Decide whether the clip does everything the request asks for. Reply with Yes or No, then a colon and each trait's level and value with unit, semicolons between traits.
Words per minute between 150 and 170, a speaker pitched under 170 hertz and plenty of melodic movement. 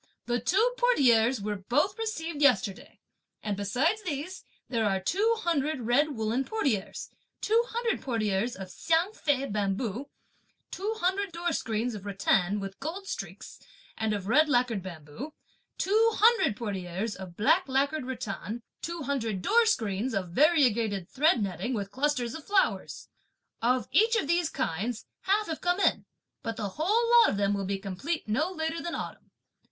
No: average, 160 wpm; very high, 260 Hz; wide, 8.6 semitones